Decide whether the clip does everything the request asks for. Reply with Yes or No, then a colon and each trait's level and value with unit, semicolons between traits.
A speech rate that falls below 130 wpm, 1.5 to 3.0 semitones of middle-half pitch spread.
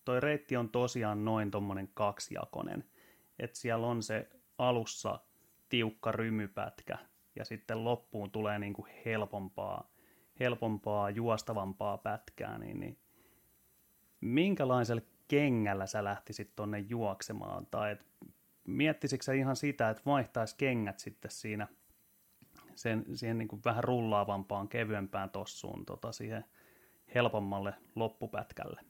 Yes: average, 110 wpm; average, 2.7 semitones